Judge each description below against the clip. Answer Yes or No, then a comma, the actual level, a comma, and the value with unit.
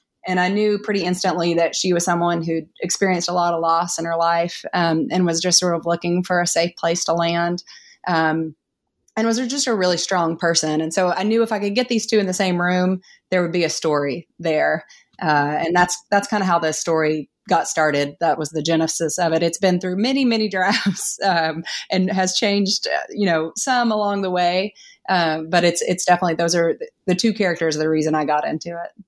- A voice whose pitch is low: No, medium, 175 Hz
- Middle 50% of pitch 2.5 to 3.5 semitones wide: Yes, average, 3.0 semitones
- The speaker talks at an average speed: No, fast, 225 wpm